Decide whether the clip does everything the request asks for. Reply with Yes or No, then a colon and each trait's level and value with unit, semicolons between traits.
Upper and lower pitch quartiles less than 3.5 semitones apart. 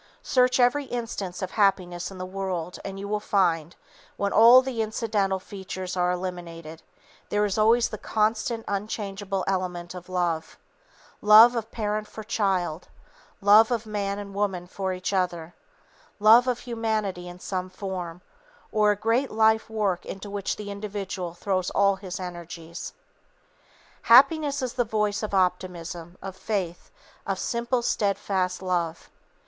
Yes: average, 3.1 semitones